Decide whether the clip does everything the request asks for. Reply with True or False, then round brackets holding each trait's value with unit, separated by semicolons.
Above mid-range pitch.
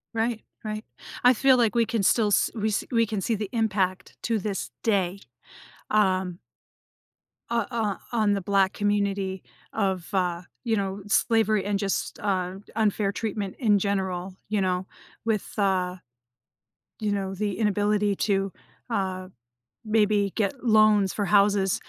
True (205 Hz)